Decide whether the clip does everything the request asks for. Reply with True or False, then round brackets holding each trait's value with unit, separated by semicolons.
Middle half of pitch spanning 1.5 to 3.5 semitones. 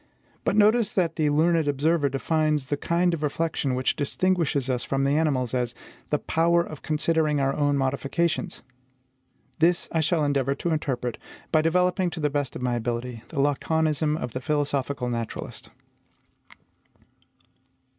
True (3.2 semitones)